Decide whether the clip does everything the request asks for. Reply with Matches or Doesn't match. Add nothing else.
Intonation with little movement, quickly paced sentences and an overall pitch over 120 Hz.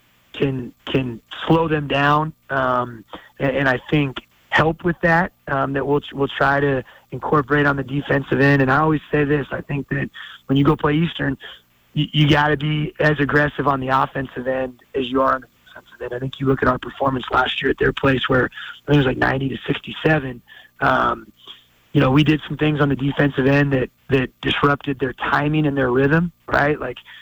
Matches